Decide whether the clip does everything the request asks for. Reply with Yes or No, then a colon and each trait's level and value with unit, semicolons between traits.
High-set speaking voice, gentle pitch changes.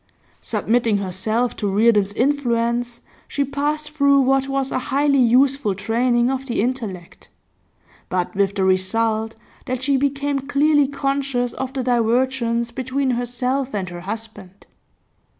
No: high, 245 Hz; average, 3.6 semitones